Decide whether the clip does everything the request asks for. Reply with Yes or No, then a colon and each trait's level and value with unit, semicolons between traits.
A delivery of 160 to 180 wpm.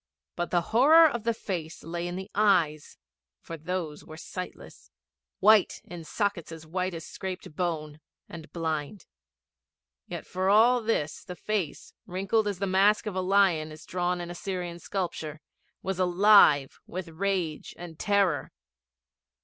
No: average, 150 wpm